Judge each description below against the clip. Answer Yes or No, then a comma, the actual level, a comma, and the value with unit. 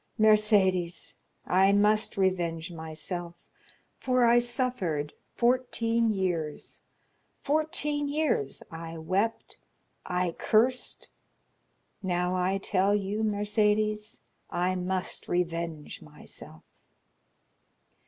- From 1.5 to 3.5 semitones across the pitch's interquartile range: No, average, 4.2 semitones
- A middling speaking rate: No, slow, 80 wpm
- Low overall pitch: No, high, 195 Hz